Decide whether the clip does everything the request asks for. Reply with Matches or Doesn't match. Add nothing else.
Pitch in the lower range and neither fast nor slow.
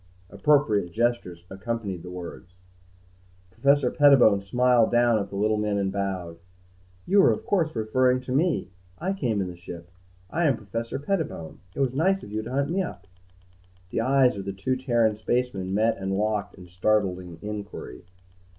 Matches